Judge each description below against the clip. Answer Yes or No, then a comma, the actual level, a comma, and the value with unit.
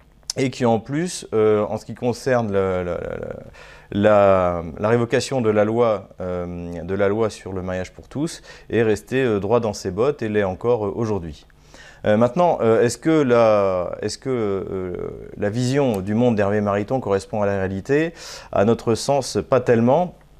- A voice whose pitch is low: Yes, low, 105 Hz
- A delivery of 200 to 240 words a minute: No, average, 180 wpm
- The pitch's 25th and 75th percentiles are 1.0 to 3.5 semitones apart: No, average, 4.0 semitones